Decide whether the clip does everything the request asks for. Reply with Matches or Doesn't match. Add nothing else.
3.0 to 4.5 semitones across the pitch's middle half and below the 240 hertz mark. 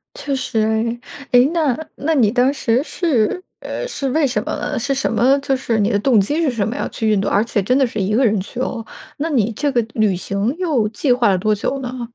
Doesn't match